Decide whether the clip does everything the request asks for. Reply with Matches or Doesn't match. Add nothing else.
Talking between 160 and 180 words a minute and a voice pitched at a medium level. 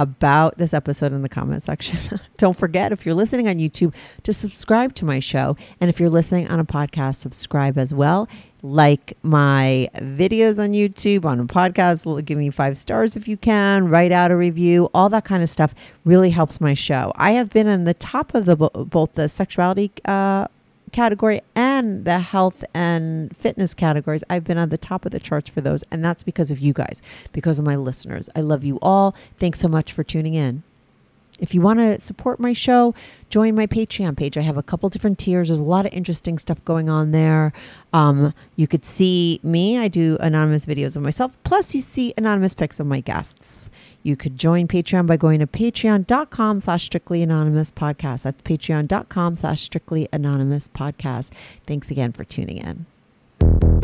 Doesn't match